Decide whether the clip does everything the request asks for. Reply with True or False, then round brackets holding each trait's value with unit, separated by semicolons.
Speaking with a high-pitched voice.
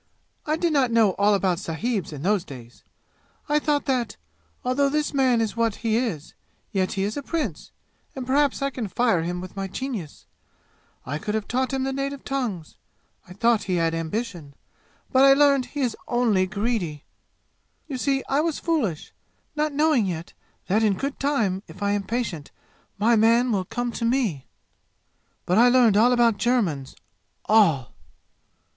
True (230 Hz)